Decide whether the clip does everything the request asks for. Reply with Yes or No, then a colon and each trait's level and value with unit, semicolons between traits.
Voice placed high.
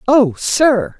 Yes: very high, 260 Hz